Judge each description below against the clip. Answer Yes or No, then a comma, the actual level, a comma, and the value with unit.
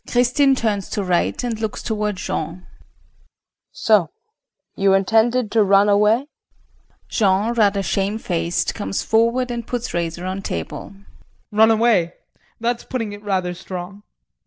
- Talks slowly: Yes, slow, 130 wpm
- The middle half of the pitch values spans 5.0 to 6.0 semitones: No, average, 3.3 semitones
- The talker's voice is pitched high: Yes, high, 210 Hz